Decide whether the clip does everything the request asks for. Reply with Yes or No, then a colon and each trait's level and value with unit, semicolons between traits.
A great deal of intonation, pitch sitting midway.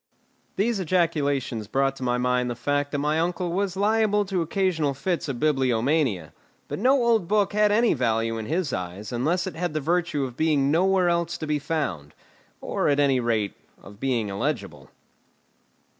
Yes: wide, 6.4 semitones; medium, 150 Hz